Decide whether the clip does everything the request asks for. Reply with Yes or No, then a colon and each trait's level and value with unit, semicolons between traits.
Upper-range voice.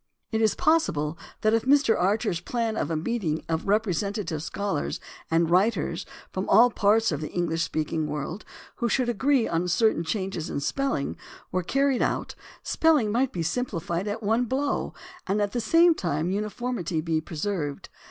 Yes: high, 200 Hz